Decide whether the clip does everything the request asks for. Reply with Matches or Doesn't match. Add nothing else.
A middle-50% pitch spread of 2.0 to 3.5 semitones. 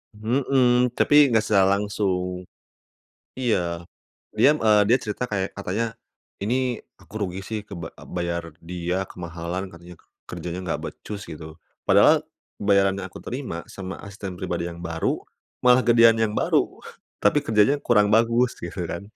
Doesn't match